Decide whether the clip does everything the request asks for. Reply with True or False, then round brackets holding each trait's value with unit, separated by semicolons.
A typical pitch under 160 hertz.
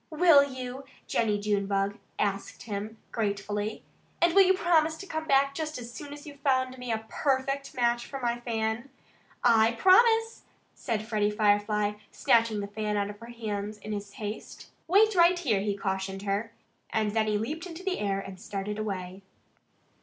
False (225 Hz)